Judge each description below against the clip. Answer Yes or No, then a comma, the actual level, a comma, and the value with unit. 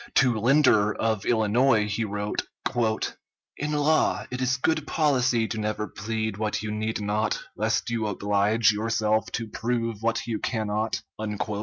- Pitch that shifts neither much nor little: No, narrow, 2.3 semitones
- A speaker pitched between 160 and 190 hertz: No, low, 110 Hz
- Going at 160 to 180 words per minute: No, average, 145 wpm